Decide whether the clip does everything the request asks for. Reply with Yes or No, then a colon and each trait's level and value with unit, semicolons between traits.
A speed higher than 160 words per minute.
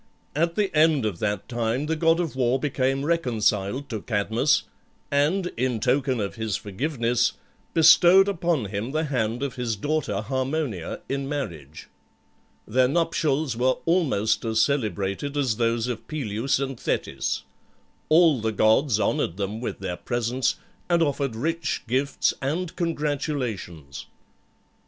No: average, 140 wpm